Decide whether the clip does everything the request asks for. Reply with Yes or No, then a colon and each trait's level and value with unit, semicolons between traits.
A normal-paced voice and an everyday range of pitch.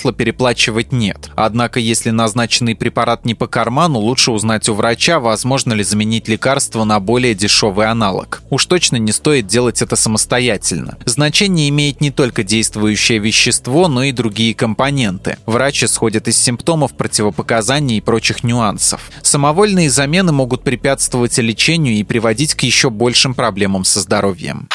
Yes: average, 145 wpm; average, 3.4 semitones